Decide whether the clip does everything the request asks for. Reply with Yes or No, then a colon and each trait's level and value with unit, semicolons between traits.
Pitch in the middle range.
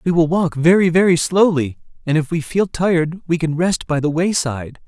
Yes: medium, 165 Hz